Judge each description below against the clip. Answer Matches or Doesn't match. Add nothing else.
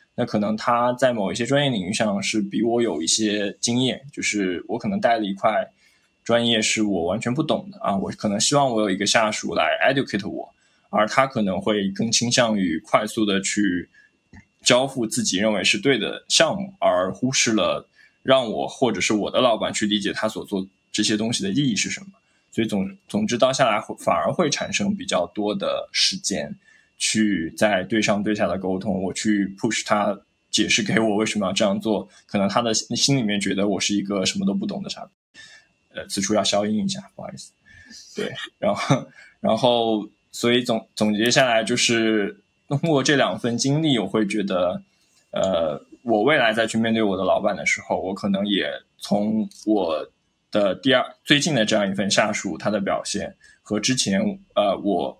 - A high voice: Doesn't match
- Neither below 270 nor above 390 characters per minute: Matches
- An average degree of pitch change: Matches